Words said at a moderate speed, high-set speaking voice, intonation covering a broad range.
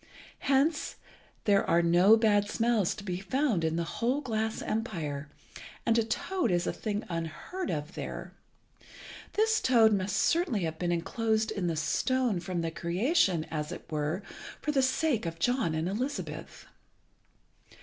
Yes: average, 155 wpm; high, 205 Hz; wide, 6.3 semitones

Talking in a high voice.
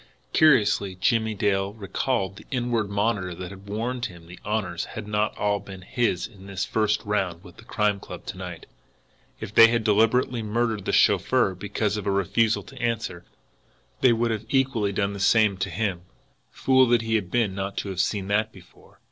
No: low, 105 Hz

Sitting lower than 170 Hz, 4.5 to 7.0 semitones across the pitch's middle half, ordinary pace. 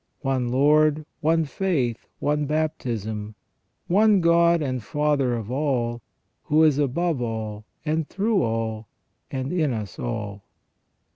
No: medium, 140 Hz; average, 5.2 semitones; slow, 125 wpm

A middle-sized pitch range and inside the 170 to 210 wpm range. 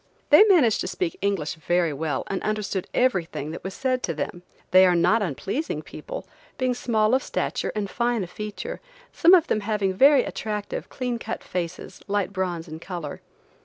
No: wide, 5.9 semitones; average, 180 wpm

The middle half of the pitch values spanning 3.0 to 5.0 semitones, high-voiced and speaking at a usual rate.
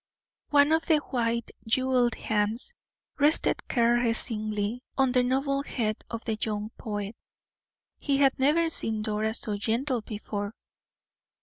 No: average, 3.9 semitones; high, 235 Hz; slow, 125 wpm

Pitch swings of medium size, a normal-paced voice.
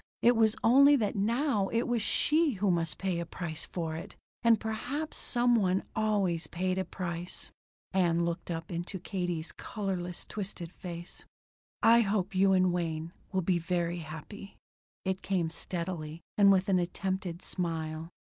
Yes: average, 3.5 semitones; average, 160 wpm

